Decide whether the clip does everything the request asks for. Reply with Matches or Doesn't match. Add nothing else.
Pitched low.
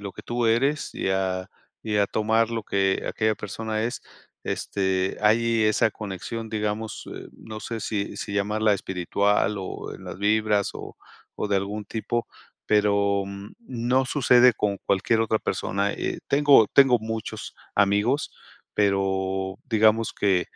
Matches